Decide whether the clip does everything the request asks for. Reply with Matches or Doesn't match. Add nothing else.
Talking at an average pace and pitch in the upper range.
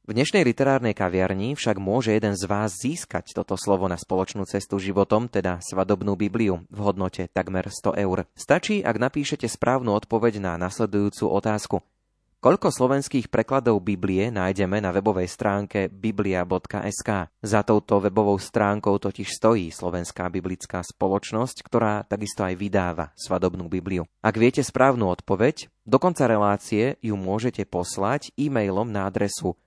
Doesn't match